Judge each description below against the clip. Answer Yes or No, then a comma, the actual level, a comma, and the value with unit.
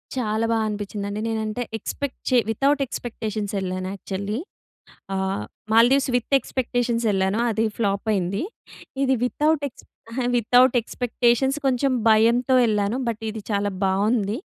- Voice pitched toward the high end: Yes, high, 225 Hz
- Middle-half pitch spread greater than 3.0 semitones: Yes, average, 3.4 semitones